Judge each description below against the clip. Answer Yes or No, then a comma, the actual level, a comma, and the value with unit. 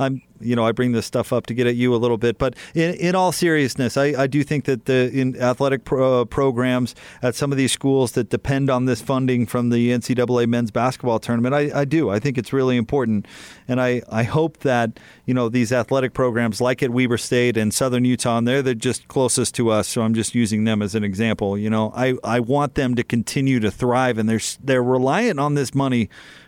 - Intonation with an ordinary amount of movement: No, narrow, 2.2 semitones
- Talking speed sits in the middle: No, fast, 235 wpm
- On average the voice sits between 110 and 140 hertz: Yes, low, 125 Hz